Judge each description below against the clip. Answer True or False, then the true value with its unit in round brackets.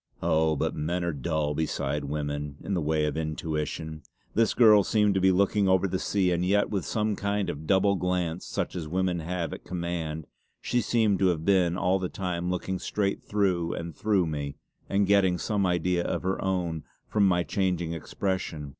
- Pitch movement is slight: False (3.5 semitones)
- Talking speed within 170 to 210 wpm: True (190 wpm)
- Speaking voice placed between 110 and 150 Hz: False (90 Hz)